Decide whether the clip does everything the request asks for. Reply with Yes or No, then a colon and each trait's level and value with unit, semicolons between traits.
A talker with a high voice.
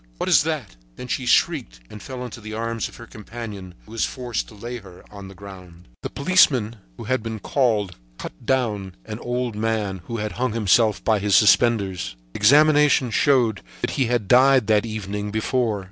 No: low, 110 Hz